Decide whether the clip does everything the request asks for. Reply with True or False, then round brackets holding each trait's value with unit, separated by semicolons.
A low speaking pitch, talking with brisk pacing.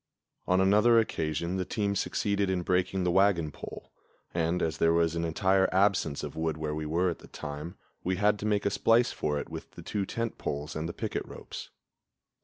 True (90 Hz; 210 wpm)